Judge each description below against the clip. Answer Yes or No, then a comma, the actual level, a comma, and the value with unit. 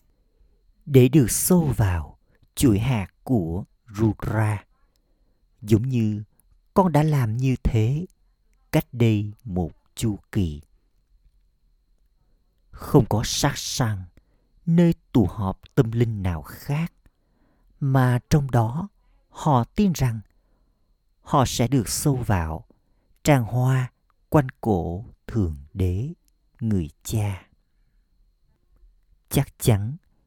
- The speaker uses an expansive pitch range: Yes, wide, 6.5 semitones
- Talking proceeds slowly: Yes, slow, 105 wpm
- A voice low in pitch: Yes, low, 110 Hz